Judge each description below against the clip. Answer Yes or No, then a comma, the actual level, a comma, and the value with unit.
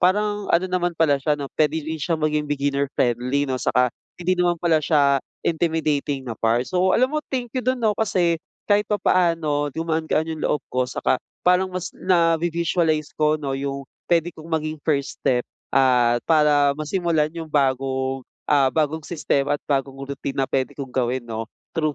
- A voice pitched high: No, medium, 155 Hz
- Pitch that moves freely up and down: No, average, 3.7 semitones